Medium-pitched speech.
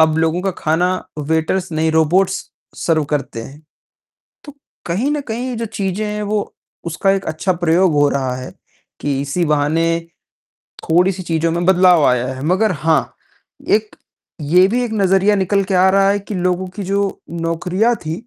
Yes: medium, 180 Hz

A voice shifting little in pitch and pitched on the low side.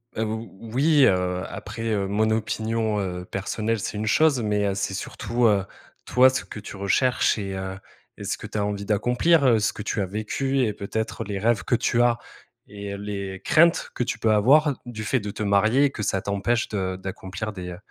No: average, 3.1 semitones; low, 105 Hz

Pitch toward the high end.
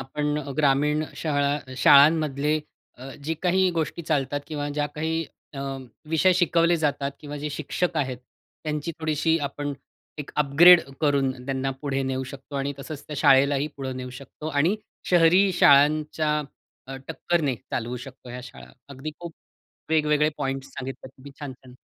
No: medium, 145 Hz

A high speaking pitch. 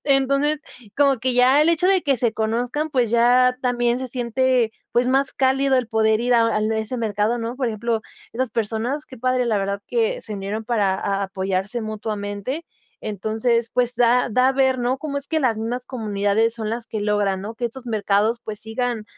Yes: high, 235 Hz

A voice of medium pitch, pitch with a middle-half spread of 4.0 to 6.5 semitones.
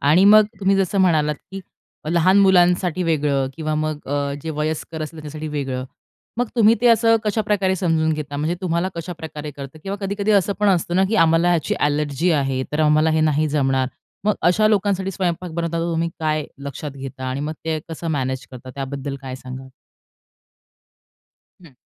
Yes: medium, 160 Hz; average, 4.3 semitones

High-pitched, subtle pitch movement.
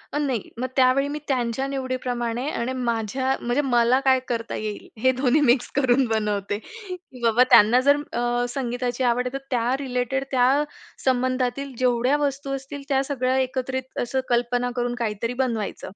Yes: very high, 255 Hz; narrow, 1.9 semitones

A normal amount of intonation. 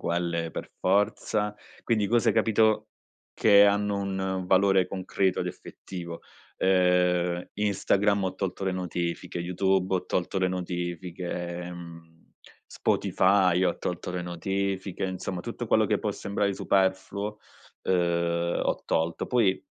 No: narrow, 2.0 semitones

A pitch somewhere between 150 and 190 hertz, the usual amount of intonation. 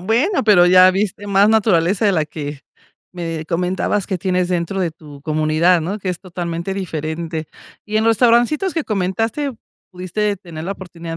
Yes: medium, 185 Hz; average, 3.9 semitones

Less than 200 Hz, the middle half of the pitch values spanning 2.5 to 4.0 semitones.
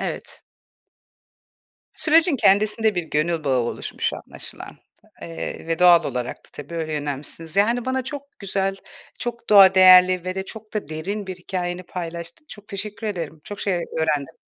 No: medium, 185 Hz; average, 4.4 semitones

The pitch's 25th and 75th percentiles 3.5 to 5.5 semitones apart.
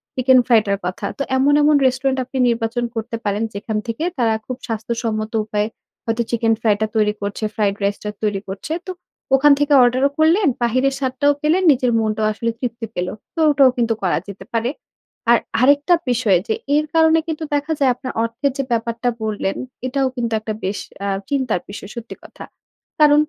Yes: average, 4.0 semitones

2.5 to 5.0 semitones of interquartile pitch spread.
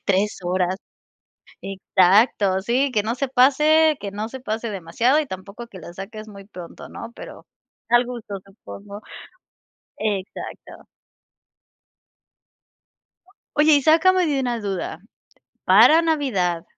No: wide, 5.4 semitones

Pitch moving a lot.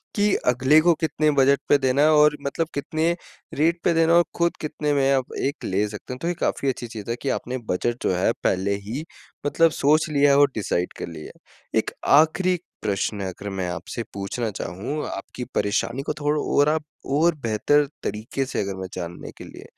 Yes: wide, 6.4 semitones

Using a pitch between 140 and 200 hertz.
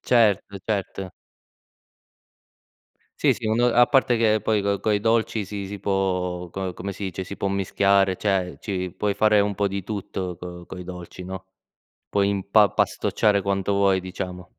No: low, 100 Hz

